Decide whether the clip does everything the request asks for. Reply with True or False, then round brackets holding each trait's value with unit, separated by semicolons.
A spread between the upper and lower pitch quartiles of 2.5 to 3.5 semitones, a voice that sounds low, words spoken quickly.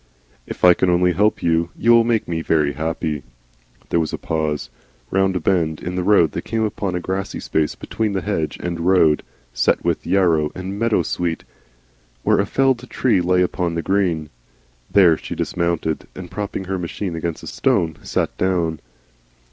False (3.1 semitones; 90 Hz; 180 wpm)